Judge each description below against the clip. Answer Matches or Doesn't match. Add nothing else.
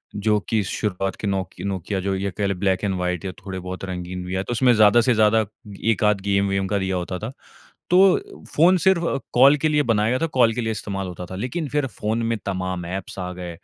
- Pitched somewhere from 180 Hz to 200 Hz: Doesn't match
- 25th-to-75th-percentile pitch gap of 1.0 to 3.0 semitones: Doesn't match